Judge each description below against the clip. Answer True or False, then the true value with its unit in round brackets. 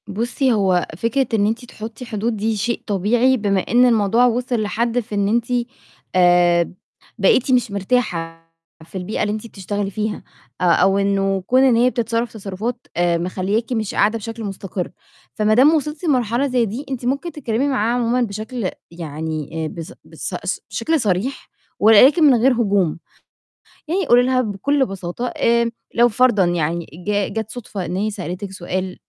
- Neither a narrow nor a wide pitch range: True (4.1 semitones)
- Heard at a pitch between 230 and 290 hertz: False (220 Hz)